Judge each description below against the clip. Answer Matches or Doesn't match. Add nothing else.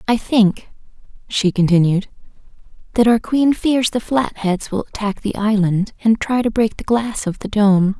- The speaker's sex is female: Matches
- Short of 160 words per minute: Doesn't match